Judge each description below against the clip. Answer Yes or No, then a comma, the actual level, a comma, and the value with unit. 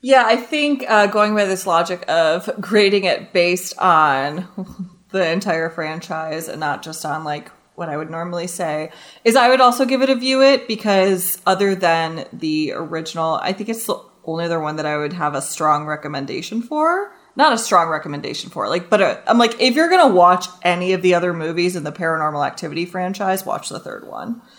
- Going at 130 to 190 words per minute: No, fast, 205 wpm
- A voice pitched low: No, medium, 180 Hz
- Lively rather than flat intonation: Yes, wide, 5.7 semitones